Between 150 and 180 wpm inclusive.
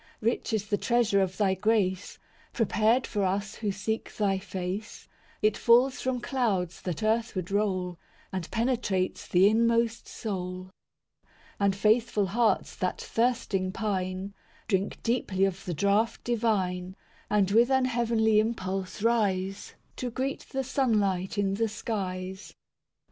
No: average, 140 wpm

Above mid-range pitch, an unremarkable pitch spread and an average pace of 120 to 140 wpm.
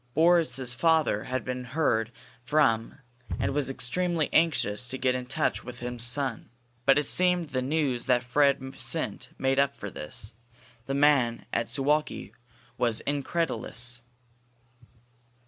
No: low, 130 Hz; average, 3.4 semitones; slow, 135 wpm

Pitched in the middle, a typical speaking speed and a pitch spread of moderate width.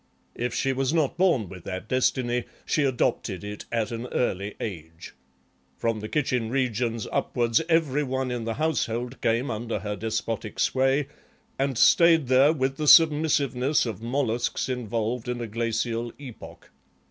No: low, 125 Hz; average, 150 wpm; average, 3.1 semitones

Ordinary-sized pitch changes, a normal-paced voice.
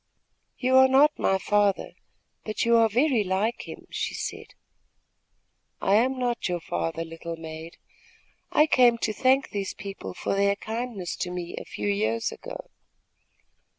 No: wide, 6.0 semitones; average, 150 wpm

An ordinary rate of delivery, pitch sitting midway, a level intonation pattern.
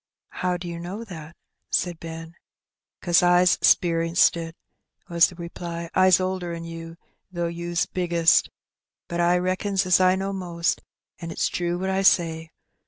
Yes: average, 160 wpm; medium, 175 Hz; narrow, 1.5 semitones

